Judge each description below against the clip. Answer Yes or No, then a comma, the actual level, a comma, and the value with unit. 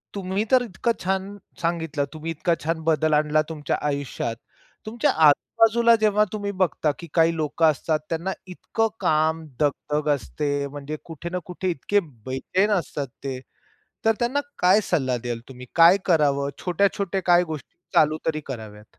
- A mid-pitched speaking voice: Yes, medium, 160 Hz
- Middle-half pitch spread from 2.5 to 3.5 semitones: No, average, 4.6 semitones